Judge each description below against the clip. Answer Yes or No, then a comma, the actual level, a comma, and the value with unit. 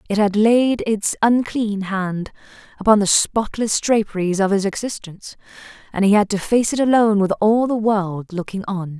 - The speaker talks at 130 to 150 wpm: No, average, 175 wpm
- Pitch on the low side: No, high, 205 Hz